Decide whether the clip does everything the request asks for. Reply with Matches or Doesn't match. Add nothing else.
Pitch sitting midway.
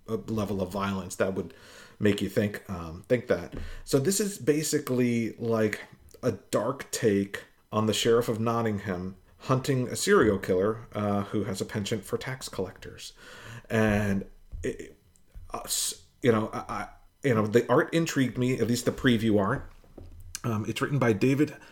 Doesn't match